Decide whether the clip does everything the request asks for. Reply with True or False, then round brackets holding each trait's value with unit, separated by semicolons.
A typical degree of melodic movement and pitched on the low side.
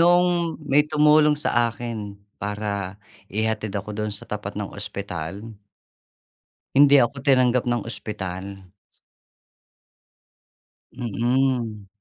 True (4.9 semitones; 110 Hz)